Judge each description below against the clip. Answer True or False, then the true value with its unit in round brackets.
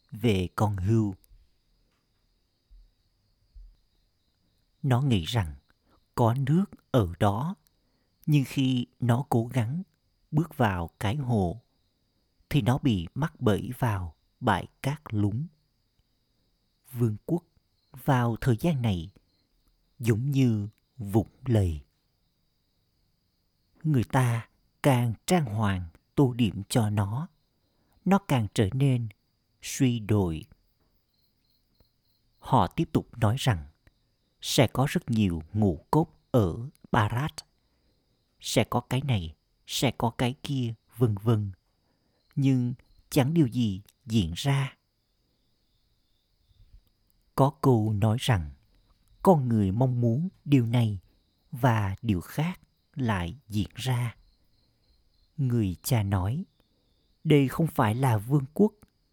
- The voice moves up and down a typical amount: True (5.0 semitones)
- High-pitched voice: False (115 Hz)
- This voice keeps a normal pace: False (110 wpm)